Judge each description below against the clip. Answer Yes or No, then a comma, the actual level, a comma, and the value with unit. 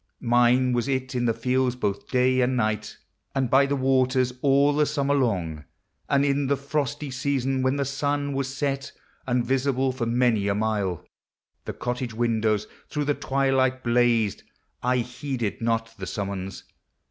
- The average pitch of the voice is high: No, low, 130 Hz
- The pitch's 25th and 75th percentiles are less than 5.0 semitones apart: Yes, average, 2.8 semitones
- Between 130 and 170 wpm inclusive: Yes, average, 160 wpm